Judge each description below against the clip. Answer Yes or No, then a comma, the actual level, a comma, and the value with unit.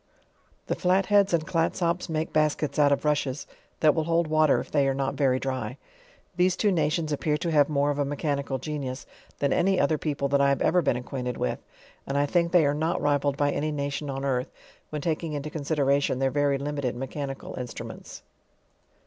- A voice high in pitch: No, medium, 145 Hz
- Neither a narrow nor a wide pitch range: No, narrow, 2.2 semitones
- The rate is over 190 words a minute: Yes, average, 200 wpm